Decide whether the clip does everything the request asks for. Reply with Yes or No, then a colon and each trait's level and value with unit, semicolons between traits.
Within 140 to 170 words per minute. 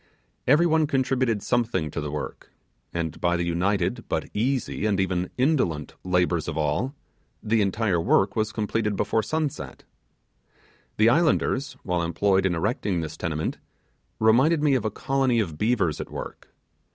Yes: average, 150 wpm